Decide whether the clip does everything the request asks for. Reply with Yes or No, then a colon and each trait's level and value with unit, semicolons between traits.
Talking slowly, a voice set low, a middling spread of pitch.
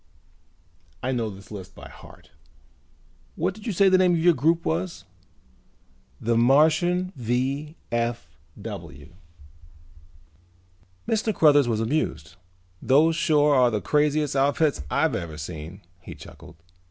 No: slow, 120 wpm; low, 130 Hz; wide, 8.3 semitones